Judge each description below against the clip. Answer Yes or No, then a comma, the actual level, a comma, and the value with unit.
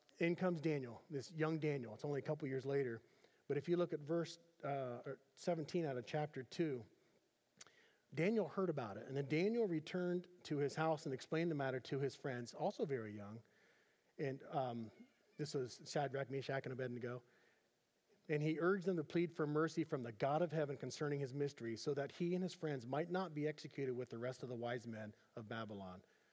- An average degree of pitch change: Yes, average, 4.4 semitones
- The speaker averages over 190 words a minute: Yes, average, 200 wpm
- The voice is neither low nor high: Yes, medium, 145 Hz